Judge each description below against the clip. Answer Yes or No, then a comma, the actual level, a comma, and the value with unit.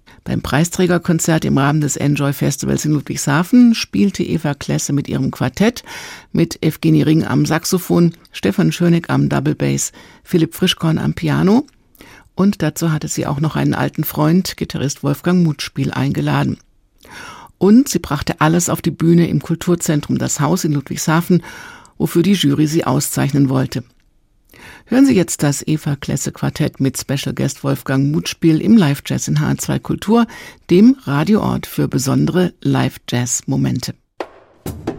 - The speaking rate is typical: Yes, average, 140 wpm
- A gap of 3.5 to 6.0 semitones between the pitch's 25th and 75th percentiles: Yes, average, 3.8 semitones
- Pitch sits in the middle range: Yes, medium, 160 Hz